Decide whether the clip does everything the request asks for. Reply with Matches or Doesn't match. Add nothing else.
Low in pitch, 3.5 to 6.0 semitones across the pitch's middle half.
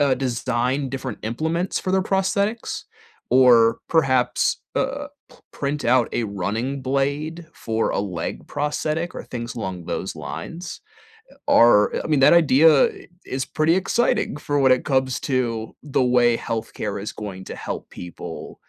Matches